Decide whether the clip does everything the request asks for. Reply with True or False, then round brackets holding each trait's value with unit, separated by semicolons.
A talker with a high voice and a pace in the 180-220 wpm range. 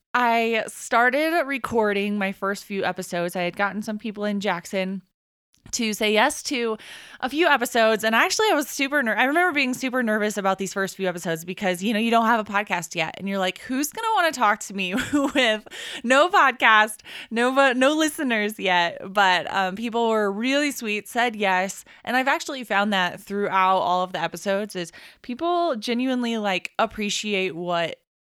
True (215 Hz; 185 wpm)